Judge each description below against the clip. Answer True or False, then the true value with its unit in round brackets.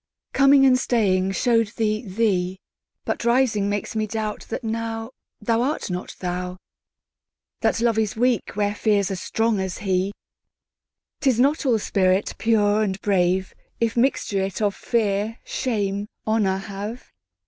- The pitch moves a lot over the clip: False (3.0 semitones)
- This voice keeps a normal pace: False (125 wpm)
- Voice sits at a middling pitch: False (210 Hz)